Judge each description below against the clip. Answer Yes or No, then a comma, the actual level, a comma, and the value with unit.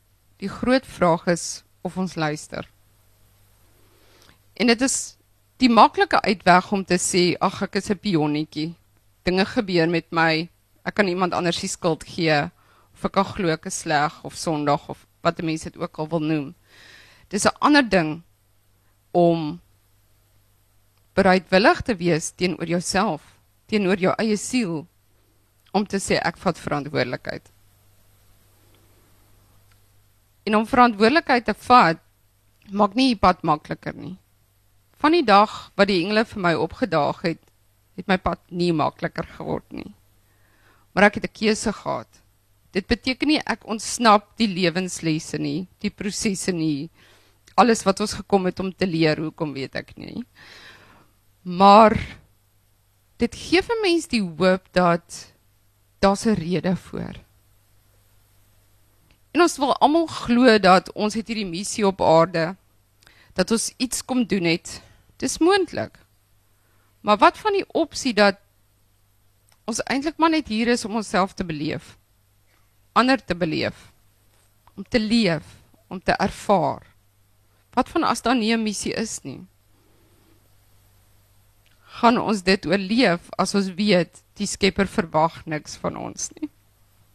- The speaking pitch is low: No, medium, 165 Hz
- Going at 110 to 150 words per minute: Yes, average, 140 wpm